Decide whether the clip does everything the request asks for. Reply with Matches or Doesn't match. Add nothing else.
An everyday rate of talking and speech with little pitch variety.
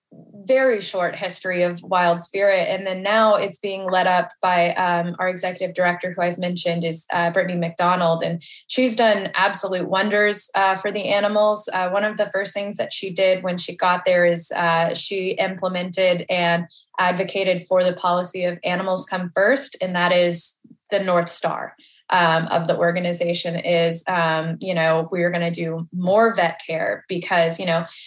Matches